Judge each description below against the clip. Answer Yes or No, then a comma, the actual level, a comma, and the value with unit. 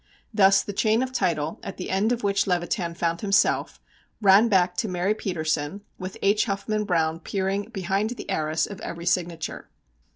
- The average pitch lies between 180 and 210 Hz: Yes, high, 190 Hz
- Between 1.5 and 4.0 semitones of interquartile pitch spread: Yes, average, 3.1 semitones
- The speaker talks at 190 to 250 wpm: No, average, 170 wpm